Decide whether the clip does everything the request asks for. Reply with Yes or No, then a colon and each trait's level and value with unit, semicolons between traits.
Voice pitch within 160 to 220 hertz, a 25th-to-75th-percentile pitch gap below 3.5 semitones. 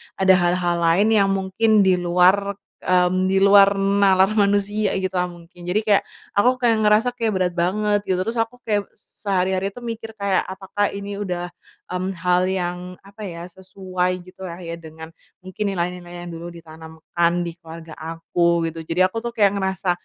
Yes: medium, 185 Hz; narrow, 2.4 semitones